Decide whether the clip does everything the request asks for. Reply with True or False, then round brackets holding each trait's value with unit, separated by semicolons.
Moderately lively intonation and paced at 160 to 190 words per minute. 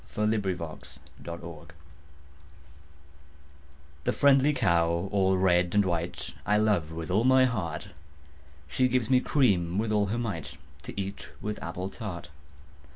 False (4.5 semitones; 135 wpm)